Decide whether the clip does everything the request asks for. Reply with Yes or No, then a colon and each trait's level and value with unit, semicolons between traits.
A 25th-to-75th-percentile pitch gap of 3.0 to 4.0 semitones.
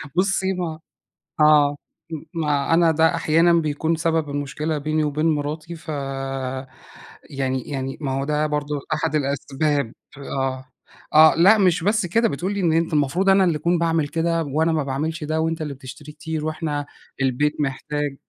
No: narrow, 2.4 semitones